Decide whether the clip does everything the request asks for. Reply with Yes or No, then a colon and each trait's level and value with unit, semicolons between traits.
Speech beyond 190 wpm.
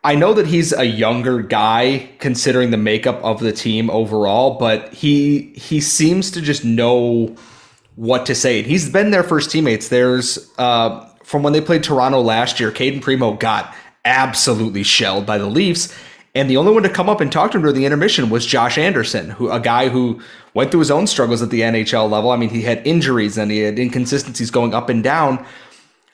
Yes: fast, 205 wpm